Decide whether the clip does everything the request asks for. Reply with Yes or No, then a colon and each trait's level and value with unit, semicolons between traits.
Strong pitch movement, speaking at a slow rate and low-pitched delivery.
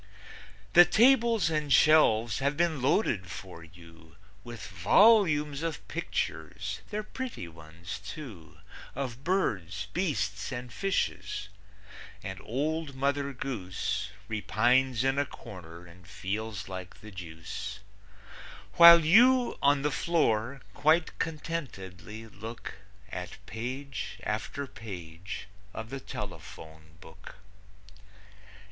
Yes: wide, 8.5 semitones; slow, 105 wpm; low, 120 Hz